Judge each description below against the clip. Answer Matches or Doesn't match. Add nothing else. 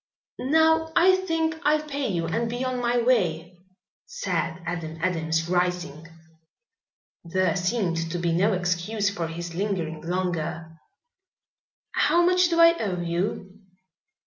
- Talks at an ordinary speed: Doesn't match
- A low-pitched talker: Doesn't match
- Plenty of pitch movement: Matches